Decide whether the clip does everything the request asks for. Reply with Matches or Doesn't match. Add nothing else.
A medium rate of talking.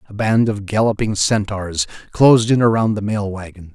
Matches